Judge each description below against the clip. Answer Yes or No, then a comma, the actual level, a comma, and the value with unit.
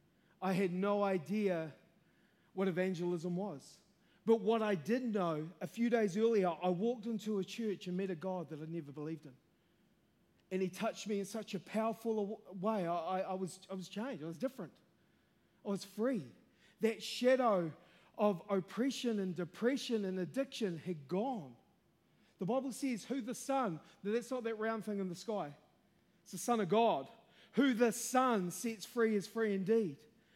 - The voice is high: Yes, high, 200 Hz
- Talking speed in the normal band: Yes, average, 175 wpm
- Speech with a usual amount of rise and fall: Yes, average, 3.8 semitones